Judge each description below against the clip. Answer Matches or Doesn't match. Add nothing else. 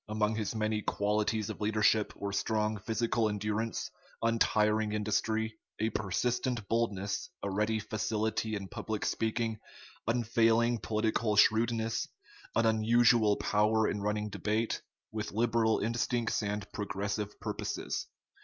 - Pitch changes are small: Matches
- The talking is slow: Matches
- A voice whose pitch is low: Matches